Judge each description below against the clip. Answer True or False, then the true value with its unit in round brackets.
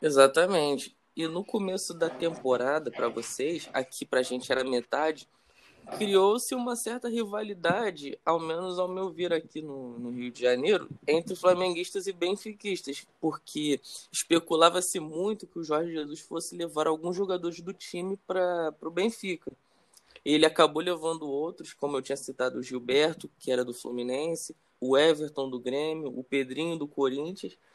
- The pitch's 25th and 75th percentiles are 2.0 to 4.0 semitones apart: False (4.7 semitones)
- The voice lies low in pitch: False (165 Hz)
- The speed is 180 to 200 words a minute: False (155 wpm)